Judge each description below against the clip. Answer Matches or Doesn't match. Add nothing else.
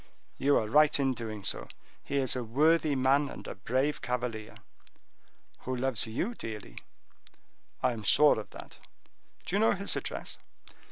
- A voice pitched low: Matches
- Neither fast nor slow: Matches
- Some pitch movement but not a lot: Matches